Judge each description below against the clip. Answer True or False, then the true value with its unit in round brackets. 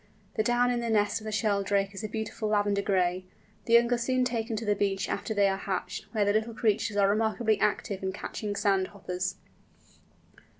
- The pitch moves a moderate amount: False (2.1 semitones)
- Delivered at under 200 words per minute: False (205 wpm)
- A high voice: True (210 Hz)